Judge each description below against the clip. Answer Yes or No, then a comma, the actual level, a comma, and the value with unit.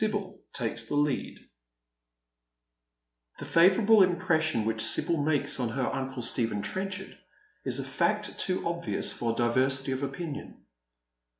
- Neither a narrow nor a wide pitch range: No, wide, 6.9 semitones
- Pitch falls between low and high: Yes, medium, 145 Hz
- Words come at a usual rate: No, slow, 125 wpm